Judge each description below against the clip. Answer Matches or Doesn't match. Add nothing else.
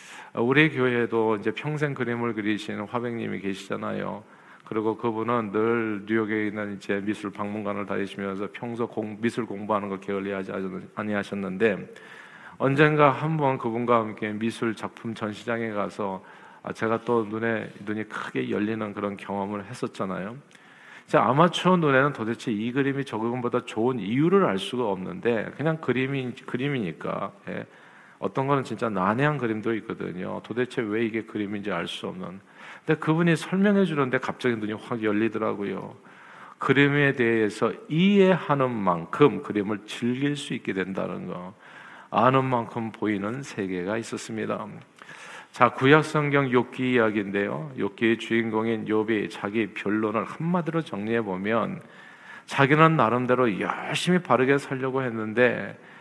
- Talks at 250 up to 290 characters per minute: Doesn't match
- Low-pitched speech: Matches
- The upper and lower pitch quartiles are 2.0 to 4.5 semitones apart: Matches